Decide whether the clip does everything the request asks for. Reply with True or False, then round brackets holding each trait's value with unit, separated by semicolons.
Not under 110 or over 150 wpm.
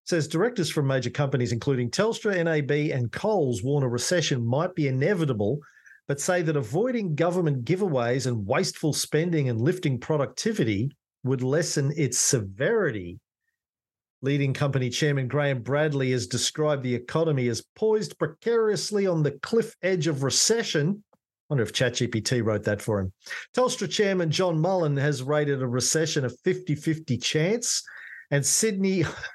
True (145 wpm)